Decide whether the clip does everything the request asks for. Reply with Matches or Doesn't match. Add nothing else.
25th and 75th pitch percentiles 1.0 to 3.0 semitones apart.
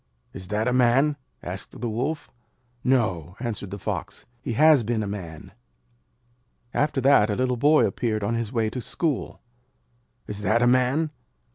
Doesn't match